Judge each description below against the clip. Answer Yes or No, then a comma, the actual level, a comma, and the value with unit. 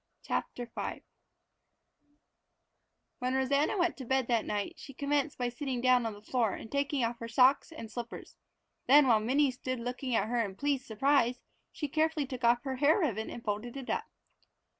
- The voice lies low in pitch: No, very high, 255 Hz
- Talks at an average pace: Yes, average, 185 wpm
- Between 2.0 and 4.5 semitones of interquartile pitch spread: Yes, average, 3.2 semitones